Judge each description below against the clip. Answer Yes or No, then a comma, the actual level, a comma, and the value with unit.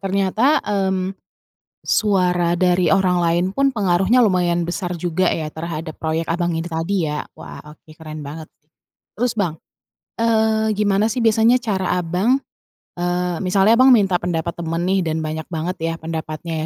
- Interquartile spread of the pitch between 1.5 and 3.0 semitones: No, average, 3.4 semitones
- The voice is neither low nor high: Yes, medium, 180 Hz